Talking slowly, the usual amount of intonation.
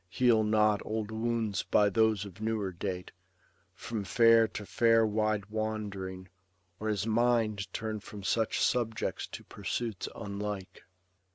No: slow, 130 wpm; narrow, 1.7 semitones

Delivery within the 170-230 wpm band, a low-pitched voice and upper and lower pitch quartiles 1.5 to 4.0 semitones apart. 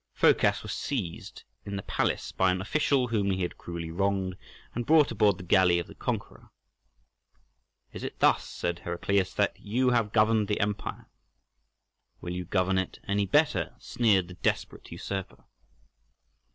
No: average, 155 wpm; low, 100 Hz; average, 3.3 semitones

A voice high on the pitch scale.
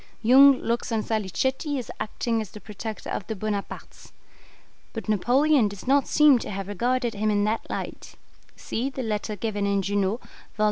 Yes: high, 220 Hz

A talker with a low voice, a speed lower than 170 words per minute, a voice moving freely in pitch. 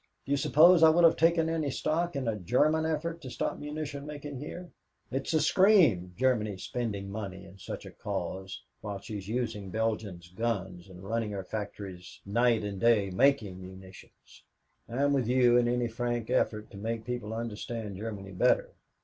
No: low, 115 Hz; average, 175 wpm; wide, 6.2 semitones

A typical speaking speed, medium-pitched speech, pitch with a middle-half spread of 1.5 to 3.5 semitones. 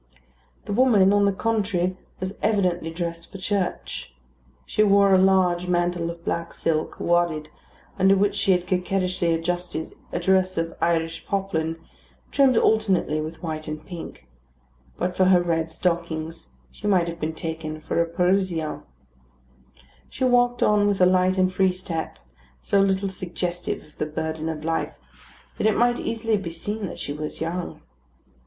Yes: average, 160 wpm; medium, 180 Hz; average, 2.9 semitones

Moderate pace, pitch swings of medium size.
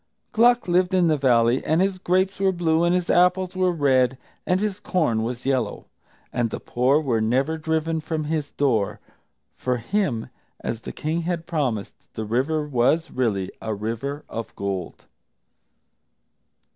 No: average, 160 wpm; wide, 6.6 semitones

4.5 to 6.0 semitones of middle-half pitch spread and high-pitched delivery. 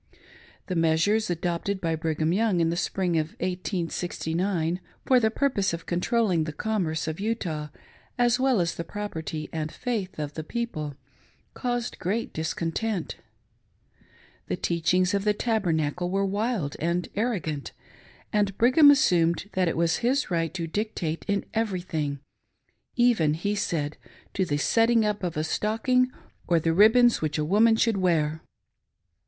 No: average, 5.2 semitones; medium, 180 Hz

